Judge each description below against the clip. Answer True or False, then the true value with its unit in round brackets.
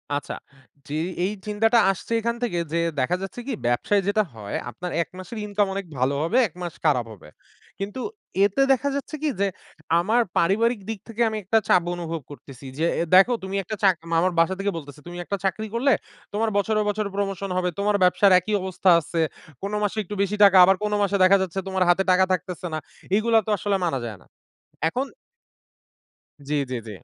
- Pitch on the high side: True (195 Hz)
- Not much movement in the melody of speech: False (3.7 semitones)